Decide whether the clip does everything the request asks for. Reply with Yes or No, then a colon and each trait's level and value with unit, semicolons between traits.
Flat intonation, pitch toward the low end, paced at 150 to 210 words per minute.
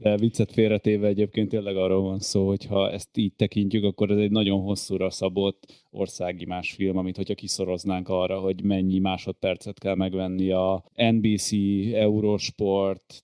Yes: narrow, 1.9 semitones; low, 100 Hz; fast, 155 wpm